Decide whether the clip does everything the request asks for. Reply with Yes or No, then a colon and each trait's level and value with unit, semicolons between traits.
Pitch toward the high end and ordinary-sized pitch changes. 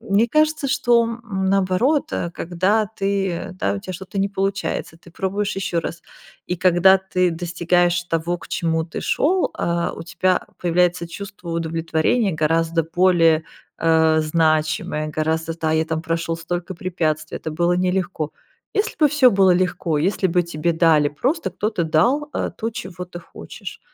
No: medium, 175 Hz; average, 3.1 semitones